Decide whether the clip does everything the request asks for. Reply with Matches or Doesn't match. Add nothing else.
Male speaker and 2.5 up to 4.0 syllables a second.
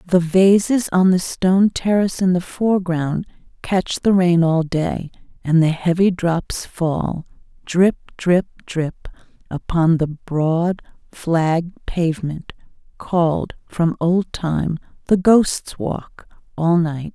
Doesn't match